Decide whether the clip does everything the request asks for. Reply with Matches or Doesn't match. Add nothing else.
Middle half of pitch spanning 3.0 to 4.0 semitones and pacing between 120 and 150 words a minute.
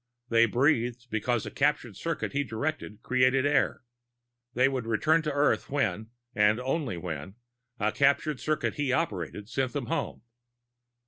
Doesn't match